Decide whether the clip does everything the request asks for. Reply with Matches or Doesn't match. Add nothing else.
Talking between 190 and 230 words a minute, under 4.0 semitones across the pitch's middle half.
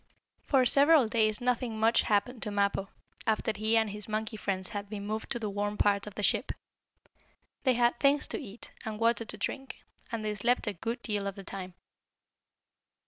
Matches